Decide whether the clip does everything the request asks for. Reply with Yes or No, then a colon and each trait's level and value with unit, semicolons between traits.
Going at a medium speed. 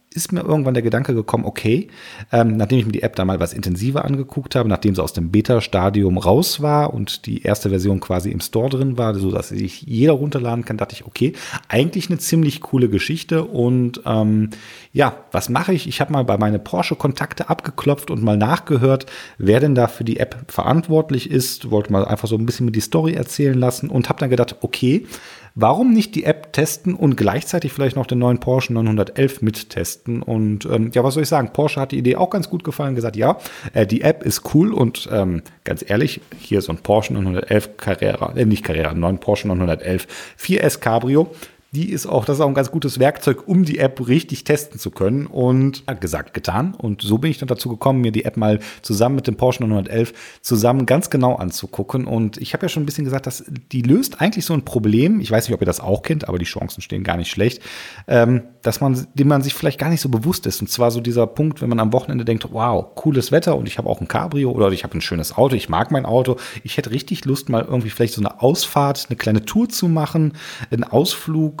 No: fast, 230 wpm